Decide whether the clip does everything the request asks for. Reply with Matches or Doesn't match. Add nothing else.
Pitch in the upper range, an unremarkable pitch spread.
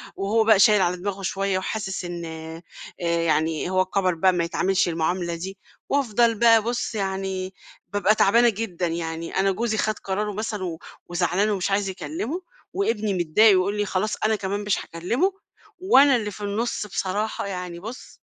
Matches